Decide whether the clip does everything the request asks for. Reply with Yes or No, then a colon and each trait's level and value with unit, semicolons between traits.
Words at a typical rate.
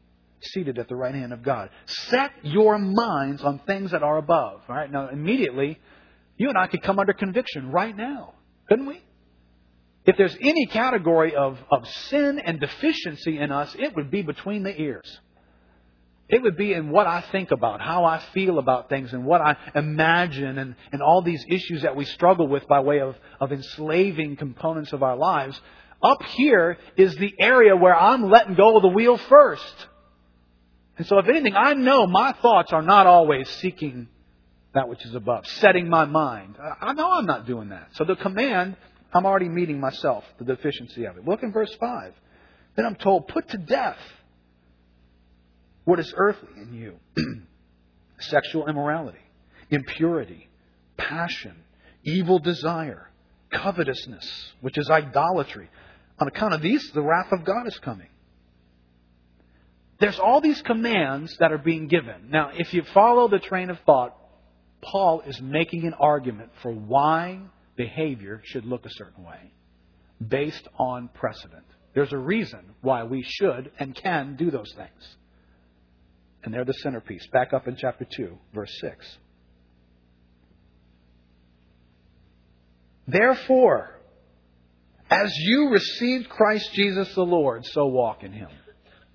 Yes: average, 155 wpm